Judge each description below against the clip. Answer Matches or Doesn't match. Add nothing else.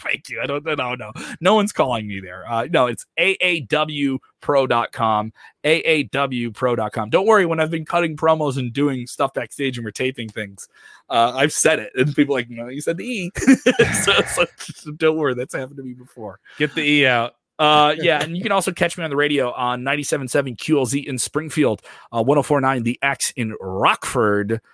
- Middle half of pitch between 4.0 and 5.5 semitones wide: Matches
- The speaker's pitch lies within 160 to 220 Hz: Doesn't match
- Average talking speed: Matches